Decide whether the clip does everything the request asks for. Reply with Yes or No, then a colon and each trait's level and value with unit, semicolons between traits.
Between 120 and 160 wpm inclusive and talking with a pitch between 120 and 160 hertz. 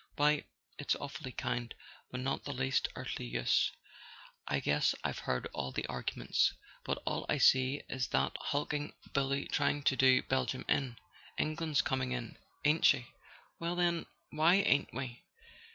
Yes: average, 150 wpm; low, 135 Hz